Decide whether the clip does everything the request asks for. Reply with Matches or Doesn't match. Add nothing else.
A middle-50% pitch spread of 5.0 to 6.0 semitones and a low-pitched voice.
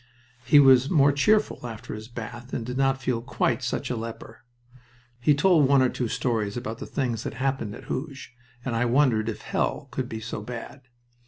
Doesn't match